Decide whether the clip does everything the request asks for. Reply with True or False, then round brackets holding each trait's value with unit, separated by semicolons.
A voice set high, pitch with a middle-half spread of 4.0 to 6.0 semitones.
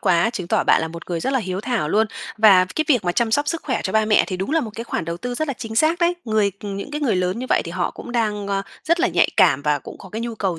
True (215 Hz; 5.2 semitones)